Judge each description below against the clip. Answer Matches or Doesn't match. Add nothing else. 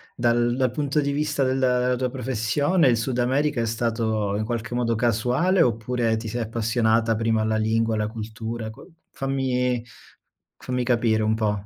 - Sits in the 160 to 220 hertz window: Doesn't match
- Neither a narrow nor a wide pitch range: Doesn't match